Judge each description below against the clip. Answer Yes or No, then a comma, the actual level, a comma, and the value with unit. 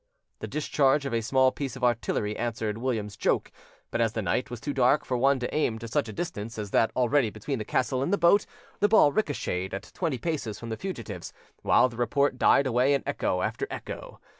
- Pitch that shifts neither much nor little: Yes, average, 4.0 semitones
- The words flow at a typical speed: No, fast, 220 wpm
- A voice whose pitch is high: No, low, 125 Hz